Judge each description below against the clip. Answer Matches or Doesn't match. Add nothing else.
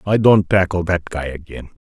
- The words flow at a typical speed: Matches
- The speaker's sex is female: Doesn't match